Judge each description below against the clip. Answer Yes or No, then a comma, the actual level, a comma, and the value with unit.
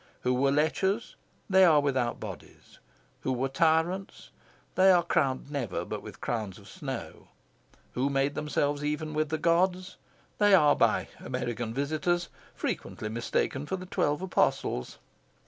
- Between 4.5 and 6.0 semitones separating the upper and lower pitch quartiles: Yes, average, 5.0 semitones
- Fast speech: No, average, 145 wpm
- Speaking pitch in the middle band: Yes, medium, 145 Hz